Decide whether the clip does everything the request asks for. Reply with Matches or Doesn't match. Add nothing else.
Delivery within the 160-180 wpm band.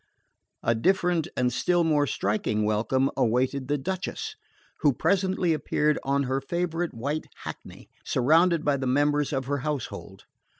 Doesn't match